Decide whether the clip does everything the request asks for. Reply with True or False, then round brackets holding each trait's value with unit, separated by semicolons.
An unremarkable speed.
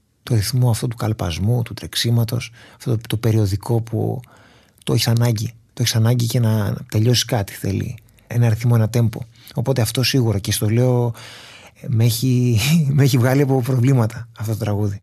False (180 wpm)